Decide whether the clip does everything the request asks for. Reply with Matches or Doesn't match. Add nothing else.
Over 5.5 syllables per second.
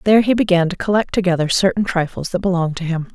Matches